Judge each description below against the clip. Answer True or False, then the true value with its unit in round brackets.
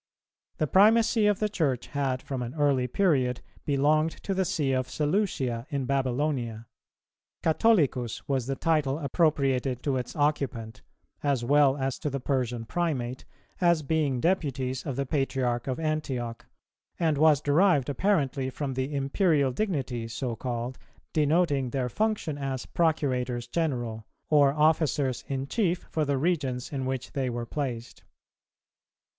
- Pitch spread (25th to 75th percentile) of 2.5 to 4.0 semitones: True (3.5 semitones)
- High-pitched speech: False (140 Hz)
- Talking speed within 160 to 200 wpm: False (140 wpm)